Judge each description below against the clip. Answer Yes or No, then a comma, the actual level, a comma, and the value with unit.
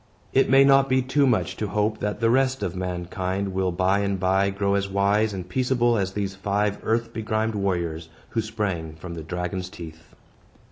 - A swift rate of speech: No, average, 190 wpm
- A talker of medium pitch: No, low, 100 Hz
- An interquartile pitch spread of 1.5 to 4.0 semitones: Yes, average, 3.4 semitones